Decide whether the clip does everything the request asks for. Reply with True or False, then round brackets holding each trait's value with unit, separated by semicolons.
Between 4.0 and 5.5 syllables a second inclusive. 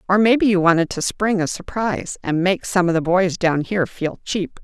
True (5.3 syllables/s)